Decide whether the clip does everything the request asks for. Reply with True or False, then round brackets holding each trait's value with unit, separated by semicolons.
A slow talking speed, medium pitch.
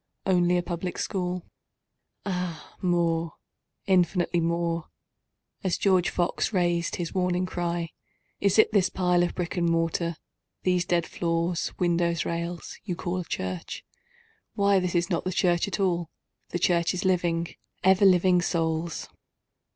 True (120 wpm; 175 Hz)